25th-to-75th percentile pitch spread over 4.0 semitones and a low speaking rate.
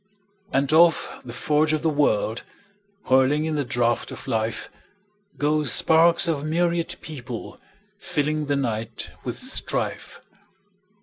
Yes: average, 4.4 semitones; slow, 110 wpm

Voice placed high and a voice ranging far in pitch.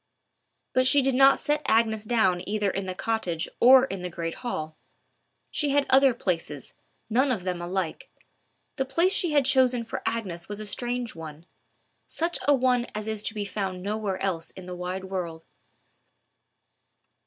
Yes: high, 215 Hz; wide, 5.9 semitones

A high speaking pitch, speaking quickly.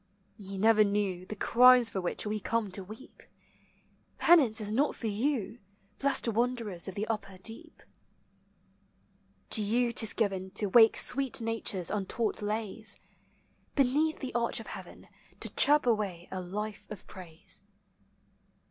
No: high, 215 Hz; average, 145 wpm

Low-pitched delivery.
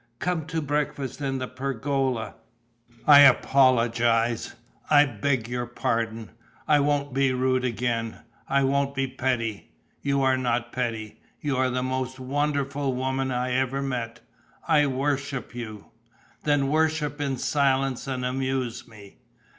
Yes: low, 130 Hz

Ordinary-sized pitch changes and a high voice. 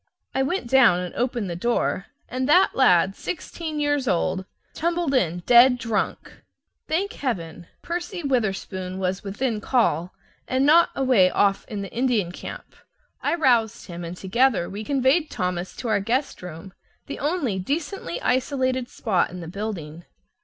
No: wide, 6.5 semitones; high, 235 Hz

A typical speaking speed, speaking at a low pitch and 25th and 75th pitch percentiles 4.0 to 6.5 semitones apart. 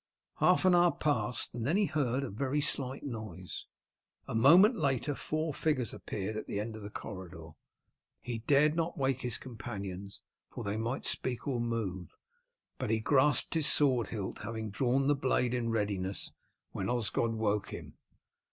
Yes: average, 170 wpm; low, 120 Hz; average, 4.6 semitones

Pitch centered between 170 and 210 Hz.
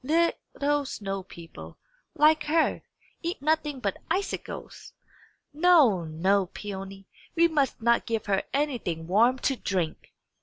No: very high, 250 Hz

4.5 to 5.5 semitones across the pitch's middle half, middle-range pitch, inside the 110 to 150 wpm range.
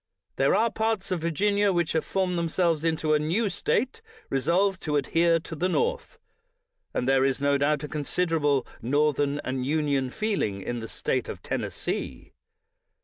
No: average, 4.8 semitones; medium, 160 Hz; average, 170 wpm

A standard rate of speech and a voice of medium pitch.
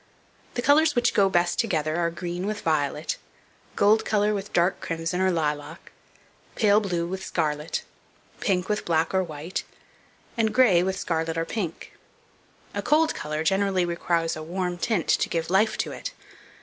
Yes: average, 160 wpm; medium, 180 Hz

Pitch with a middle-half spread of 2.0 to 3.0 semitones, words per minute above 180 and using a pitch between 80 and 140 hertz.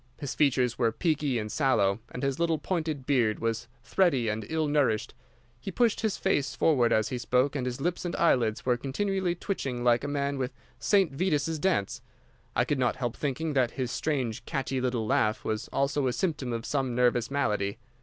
No: average, 4.3 semitones; average, 195 wpm; low, 135 Hz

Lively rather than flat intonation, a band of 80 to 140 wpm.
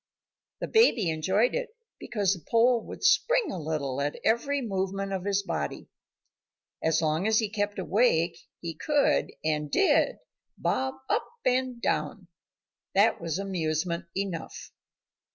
Yes: wide, 6.3 semitones; slow, 135 wpm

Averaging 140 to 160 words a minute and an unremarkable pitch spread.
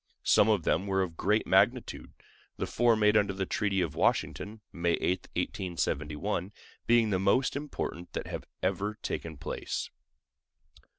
Yes: average, 145 wpm; average, 3.3 semitones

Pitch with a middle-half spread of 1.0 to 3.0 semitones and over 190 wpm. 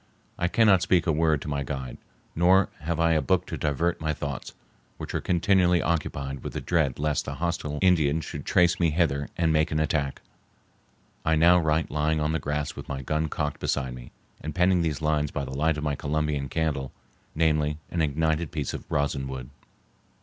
Yes: narrow, 2.6 semitones; average, 200 wpm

